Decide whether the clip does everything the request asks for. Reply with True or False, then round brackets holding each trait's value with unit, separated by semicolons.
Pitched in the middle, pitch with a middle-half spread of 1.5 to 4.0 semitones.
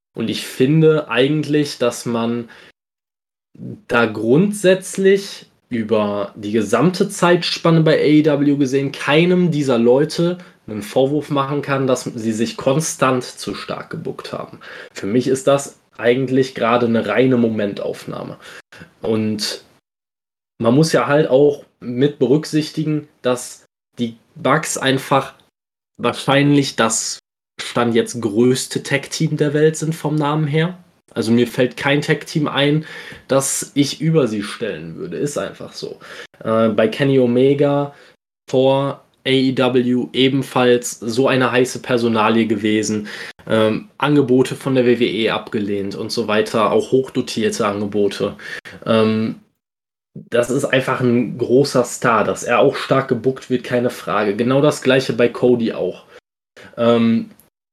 False (130 Hz; 3.7 semitones)